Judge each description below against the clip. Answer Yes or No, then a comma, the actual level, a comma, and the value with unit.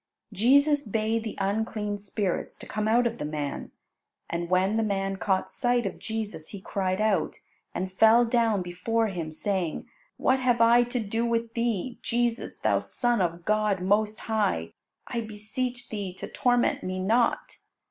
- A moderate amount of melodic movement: Yes, average, 3.5 semitones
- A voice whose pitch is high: Yes, high, 215 Hz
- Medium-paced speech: Yes, average, 165 wpm